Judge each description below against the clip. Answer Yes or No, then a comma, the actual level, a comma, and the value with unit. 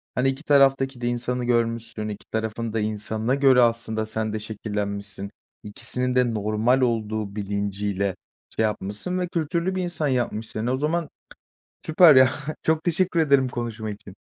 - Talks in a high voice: No, low, 115 Hz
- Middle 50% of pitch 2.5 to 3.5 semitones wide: No, average, 4.0 semitones